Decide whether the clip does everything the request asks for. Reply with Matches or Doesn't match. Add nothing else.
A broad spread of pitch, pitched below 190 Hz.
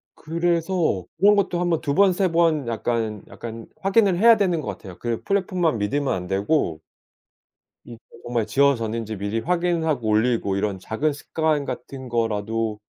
Matches